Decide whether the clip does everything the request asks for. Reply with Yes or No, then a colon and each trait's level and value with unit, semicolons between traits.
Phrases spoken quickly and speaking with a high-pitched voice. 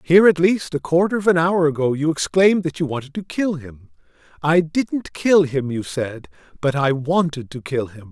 No: fast, 215 wpm; medium, 155 Hz